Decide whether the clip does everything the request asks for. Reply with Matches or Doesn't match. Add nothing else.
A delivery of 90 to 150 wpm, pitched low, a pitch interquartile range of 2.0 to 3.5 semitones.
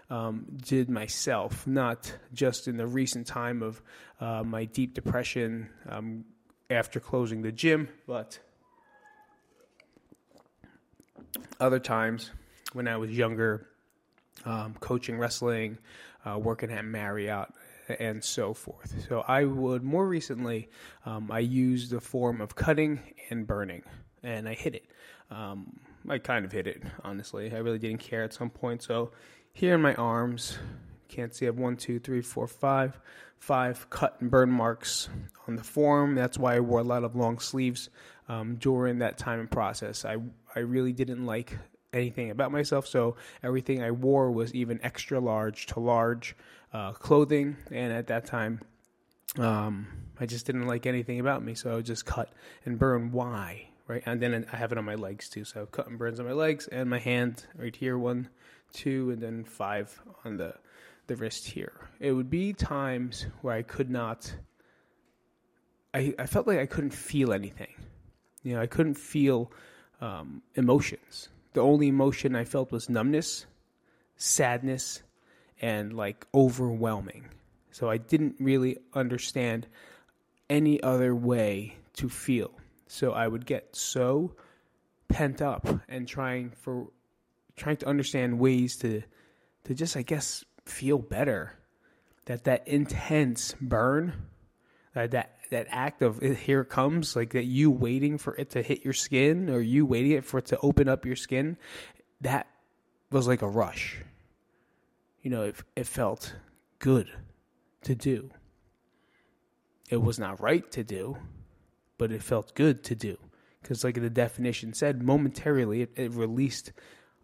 Doesn't match